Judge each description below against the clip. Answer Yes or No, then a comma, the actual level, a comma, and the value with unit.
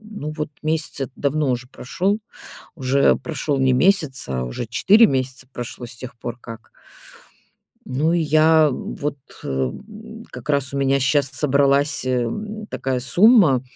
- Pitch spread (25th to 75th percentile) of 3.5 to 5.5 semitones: Yes, average, 3.9 semitones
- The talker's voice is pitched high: No, medium, 140 Hz